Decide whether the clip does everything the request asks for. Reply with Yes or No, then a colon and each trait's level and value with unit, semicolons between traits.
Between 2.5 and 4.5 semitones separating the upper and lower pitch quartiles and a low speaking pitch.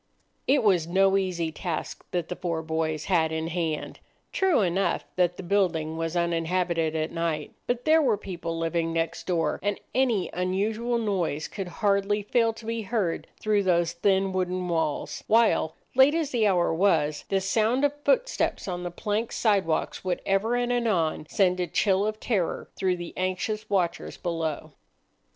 No: average, 4.2 semitones; medium, 185 Hz